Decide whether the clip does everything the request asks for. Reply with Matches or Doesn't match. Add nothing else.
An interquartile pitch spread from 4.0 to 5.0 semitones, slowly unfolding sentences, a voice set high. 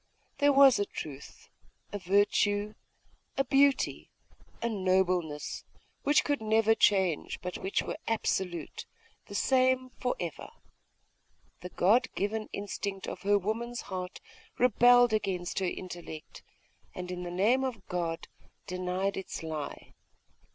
Matches